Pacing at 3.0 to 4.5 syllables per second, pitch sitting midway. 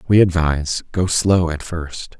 No: 4.2 syllables/s; very low, 85 Hz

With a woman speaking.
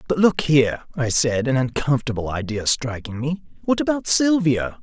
No: male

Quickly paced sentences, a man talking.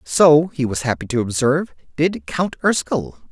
No: average, 165 wpm; male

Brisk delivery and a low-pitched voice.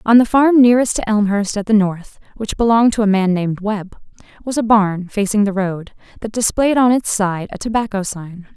No: fast, 210 wpm; high, 210 Hz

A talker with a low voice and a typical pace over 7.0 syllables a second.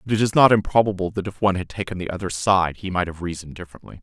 Yes: very low, 95 Hz; 7.4 syllables/s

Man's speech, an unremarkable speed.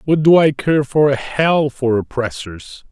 Yes: male; average, 185 wpm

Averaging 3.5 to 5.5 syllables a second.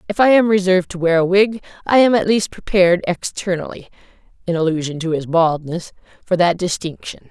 No: 5.7 syllables/s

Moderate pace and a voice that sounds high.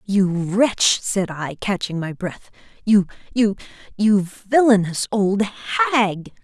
No: slow, 95 wpm; high, 200 Hz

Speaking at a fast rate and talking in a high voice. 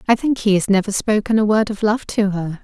Yes: fast, 275 wpm; high, 210 Hz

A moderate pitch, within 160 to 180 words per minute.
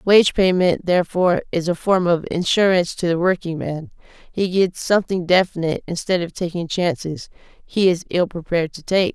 Yes: medium, 175 Hz; average, 165 wpm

